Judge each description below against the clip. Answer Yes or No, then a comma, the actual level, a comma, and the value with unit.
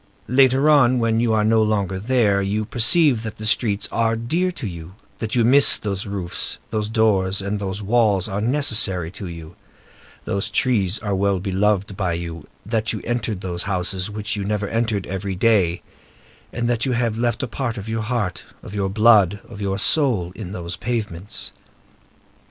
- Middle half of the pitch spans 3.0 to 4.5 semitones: Yes, average, 3.3 semitones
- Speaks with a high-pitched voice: No, low, 105 Hz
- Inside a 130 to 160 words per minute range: No, average, 185 wpm